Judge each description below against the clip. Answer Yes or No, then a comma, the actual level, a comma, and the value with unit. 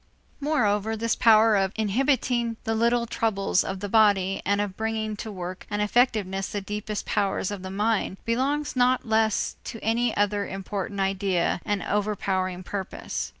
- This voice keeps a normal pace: Yes, average, 155 wpm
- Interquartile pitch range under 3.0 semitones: Yes, narrow, 2.5 semitones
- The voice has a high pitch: Yes, high, 210 Hz